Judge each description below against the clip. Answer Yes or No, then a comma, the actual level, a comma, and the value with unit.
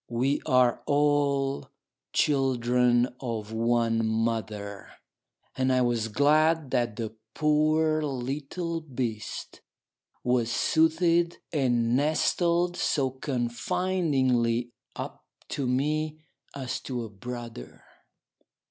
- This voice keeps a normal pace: No, slow, 95 wpm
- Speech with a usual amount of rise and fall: Yes, average, 4.3 semitones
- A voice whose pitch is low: Yes, low, 130 Hz